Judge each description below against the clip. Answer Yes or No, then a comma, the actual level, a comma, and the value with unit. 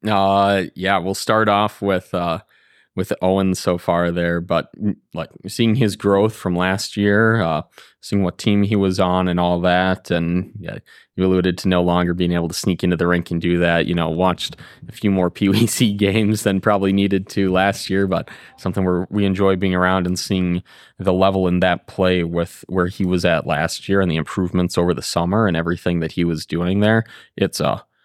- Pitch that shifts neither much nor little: No, narrow, 2.1 semitones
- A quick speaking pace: Yes, fast, 210 wpm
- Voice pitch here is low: Yes, very low, 95 Hz